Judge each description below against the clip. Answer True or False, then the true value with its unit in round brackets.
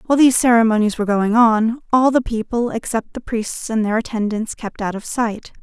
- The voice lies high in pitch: True (225 Hz)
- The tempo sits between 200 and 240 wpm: True (205 wpm)